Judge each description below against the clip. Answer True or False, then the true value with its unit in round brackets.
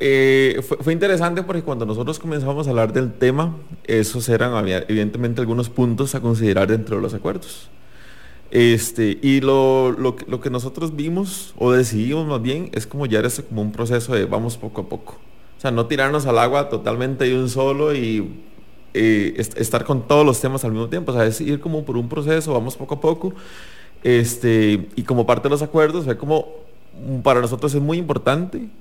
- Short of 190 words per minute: False (195 wpm)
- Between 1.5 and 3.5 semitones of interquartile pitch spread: False (4.2 semitones)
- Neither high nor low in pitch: False (130 Hz)